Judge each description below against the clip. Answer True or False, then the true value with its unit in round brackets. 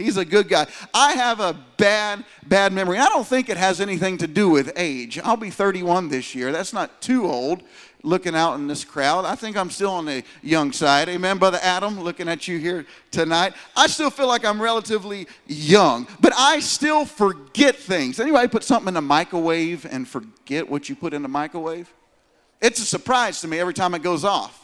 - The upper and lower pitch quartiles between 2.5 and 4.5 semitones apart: False (5.1 semitones)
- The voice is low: False (185 Hz)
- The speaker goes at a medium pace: False (210 wpm)